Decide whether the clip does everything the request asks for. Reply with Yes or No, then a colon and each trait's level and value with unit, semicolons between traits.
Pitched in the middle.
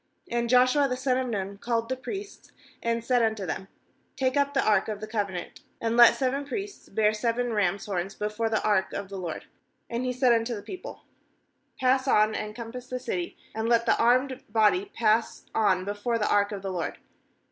No: high, 230 Hz